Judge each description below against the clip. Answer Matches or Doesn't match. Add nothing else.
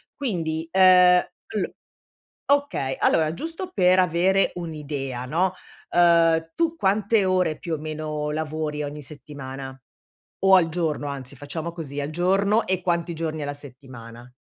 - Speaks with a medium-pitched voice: Matches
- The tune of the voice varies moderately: Matches